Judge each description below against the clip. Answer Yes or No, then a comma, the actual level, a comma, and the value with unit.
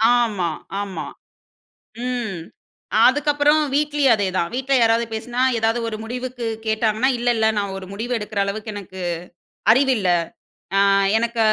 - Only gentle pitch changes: No, average, 3.5 semitones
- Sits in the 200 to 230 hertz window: Yes, high, 225 Hz